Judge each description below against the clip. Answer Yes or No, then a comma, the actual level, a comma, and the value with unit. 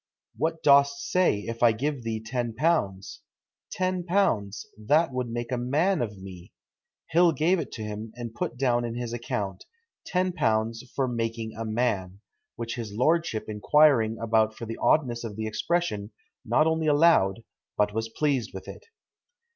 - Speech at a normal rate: Yes, average, 160 wpm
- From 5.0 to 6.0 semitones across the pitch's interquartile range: Yes, wide, 5.4 semitones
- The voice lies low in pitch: Yes, low, 120 Hz